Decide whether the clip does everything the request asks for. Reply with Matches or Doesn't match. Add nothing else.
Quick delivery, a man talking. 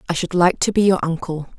Doesn't match